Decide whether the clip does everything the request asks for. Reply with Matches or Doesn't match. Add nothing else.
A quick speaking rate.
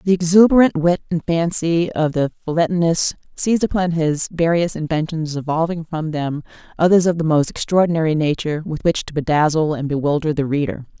Doesn't match